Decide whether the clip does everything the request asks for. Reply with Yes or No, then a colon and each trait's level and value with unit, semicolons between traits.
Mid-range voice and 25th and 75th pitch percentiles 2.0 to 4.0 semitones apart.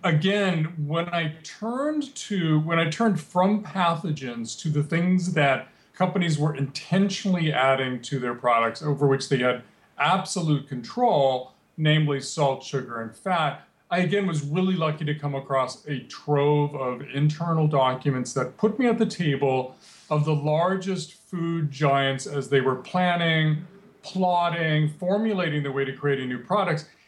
No: medium, 155 Hz; average, 4.7 semitones